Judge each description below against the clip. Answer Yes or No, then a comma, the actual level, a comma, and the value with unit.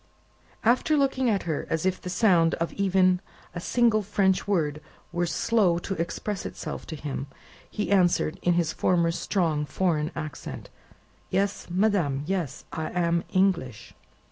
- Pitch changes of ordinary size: Yes, average, 3.3 semitones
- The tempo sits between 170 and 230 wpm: No, average, 145 wpm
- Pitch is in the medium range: Yes, medium, 180 Hz